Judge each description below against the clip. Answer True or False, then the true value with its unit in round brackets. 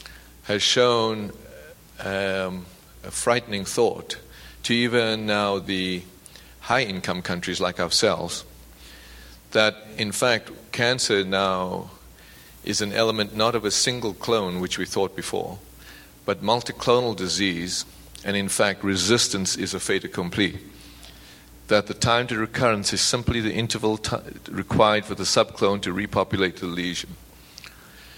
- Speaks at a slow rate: True (130 wpm)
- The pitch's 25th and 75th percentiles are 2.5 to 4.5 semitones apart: True (3.3 semitones)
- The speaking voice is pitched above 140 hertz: False (100 Hz)